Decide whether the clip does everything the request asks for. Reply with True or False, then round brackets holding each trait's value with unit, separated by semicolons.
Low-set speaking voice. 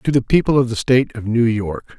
True (120 Hz)